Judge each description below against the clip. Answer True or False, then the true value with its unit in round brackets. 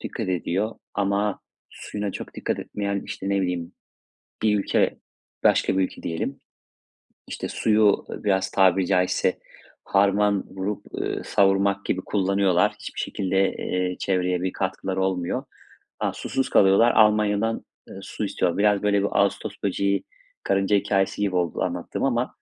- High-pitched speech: False (100 Hz)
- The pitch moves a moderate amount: False (1.5 semitones)